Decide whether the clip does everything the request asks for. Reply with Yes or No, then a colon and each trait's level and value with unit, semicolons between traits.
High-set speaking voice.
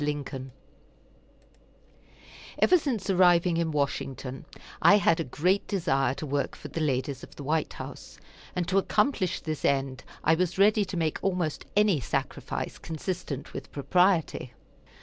No: medium, 165 Hz